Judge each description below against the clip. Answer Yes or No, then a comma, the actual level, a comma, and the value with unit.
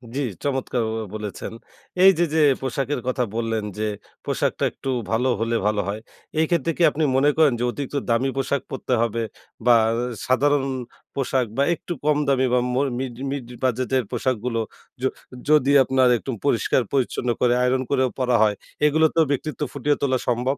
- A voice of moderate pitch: No, low, 130 Hz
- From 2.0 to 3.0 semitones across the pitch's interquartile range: Yes, average, 2.7 semitones